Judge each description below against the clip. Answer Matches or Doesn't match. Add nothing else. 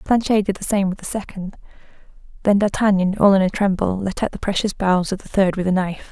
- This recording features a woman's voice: Matches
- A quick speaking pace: Matches